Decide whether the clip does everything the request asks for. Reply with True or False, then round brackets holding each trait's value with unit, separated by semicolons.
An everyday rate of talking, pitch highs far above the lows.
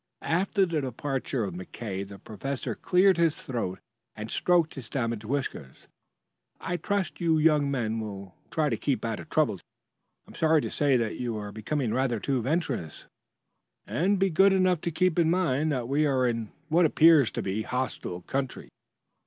True (185 wpm; 6.3 semitones)